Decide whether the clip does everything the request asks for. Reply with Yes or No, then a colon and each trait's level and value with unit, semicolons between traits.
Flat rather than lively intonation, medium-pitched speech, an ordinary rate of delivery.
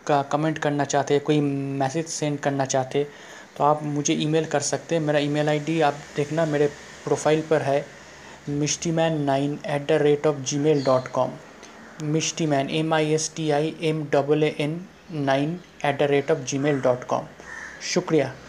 Yes: narrow, 1.6 semitones; medium, 150 Hz; average, 180 wpm